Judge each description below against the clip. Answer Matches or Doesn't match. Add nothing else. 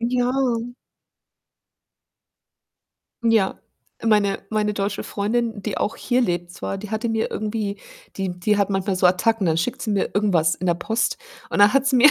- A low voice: Doesn't match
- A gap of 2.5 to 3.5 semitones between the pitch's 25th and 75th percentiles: Matches